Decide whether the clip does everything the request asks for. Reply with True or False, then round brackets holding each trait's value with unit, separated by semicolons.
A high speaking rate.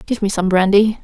True (230 wpm)